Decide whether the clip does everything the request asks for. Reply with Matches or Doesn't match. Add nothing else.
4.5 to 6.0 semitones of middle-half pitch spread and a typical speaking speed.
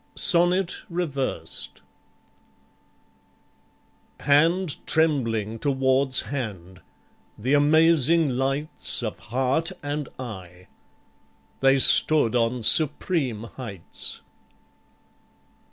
Doesn't match